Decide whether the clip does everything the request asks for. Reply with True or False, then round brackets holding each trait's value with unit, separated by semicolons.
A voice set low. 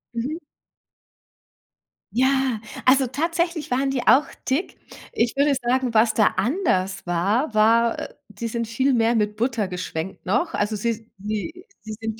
False (235 Hz)